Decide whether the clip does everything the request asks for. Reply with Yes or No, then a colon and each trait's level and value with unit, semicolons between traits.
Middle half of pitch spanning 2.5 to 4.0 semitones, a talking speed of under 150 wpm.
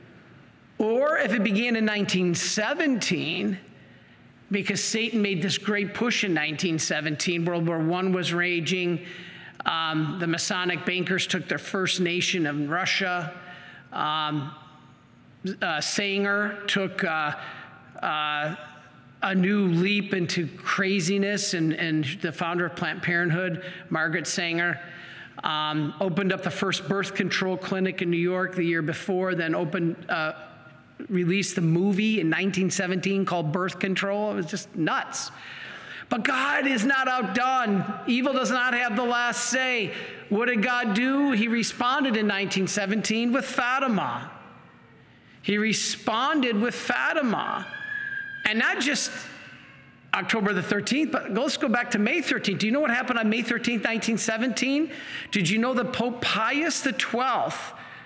No: average, 4.7 semitones; average, 140 wpm